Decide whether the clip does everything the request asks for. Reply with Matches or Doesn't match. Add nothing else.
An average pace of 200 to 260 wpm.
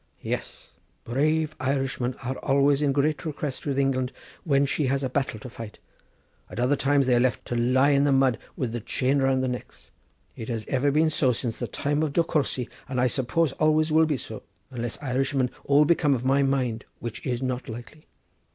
Matches